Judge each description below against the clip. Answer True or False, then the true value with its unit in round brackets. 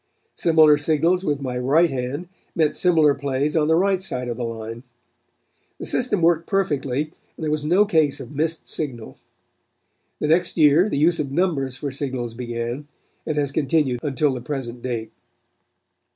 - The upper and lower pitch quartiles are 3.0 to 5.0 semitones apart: True (4.0 semitones)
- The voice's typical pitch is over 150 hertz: False (145 Hz)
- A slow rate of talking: False (165 wpm)